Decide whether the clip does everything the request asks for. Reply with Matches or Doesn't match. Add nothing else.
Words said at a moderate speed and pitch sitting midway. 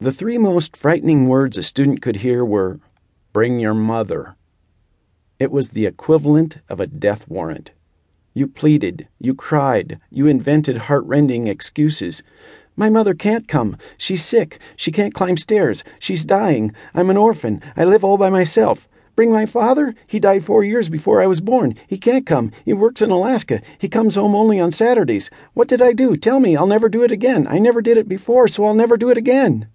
Matches